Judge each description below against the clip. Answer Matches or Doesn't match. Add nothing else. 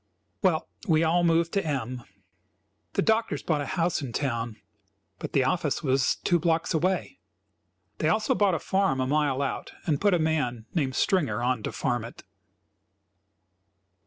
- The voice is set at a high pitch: Doesn't match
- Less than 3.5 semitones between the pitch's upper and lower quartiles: Doesn't match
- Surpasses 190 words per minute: Doesn't match